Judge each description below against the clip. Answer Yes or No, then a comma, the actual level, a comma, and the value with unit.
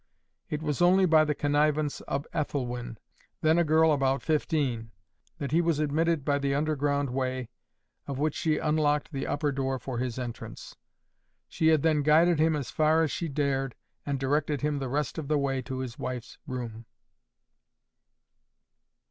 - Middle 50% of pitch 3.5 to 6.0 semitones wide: No, narrow, 2.6 semitones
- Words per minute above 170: No, average, 165 wpm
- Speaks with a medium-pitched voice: Yes, medium, 145 Hz